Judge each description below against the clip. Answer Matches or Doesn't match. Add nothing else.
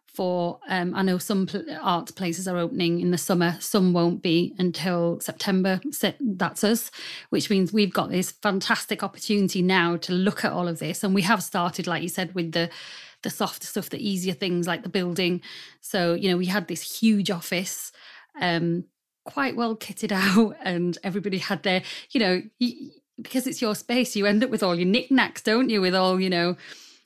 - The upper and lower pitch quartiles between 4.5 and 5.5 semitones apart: Doesn't match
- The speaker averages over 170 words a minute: Matches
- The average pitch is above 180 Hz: Matches